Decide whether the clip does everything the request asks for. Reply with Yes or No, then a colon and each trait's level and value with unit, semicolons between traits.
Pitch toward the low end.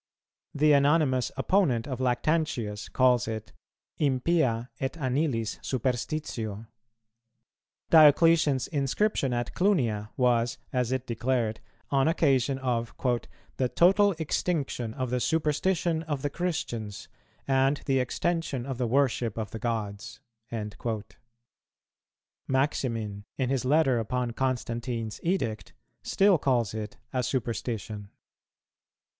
Yes: low, 130 Hz